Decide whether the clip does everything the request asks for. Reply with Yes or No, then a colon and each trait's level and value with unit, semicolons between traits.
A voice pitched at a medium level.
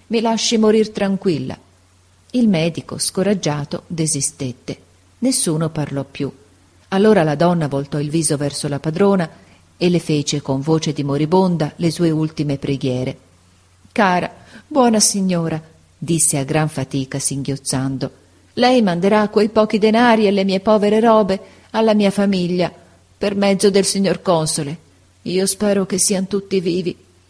Yes: medium, 170 Hz